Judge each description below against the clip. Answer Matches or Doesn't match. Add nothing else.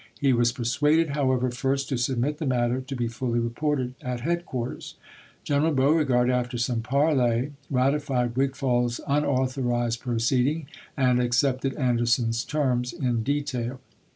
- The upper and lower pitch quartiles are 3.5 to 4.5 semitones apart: Doesn't match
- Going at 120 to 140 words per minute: Doesn't match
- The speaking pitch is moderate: Doesn't match